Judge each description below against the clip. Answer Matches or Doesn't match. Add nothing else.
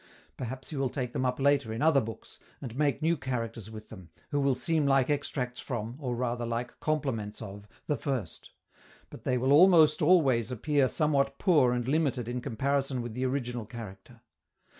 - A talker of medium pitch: Doesn't match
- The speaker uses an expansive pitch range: Doesn't match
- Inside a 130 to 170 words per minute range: Doesn't match